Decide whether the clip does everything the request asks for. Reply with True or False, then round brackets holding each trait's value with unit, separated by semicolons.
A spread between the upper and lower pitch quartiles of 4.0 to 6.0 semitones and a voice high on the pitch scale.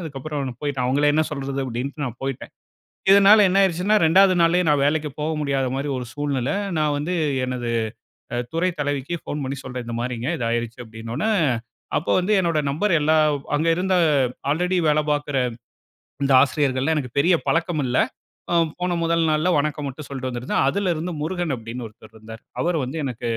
False (4.4 semitones; 145 Hz)